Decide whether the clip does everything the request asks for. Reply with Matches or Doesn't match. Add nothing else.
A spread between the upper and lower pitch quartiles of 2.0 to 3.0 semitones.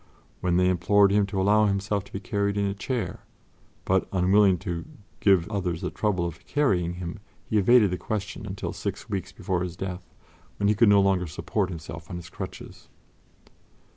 Matches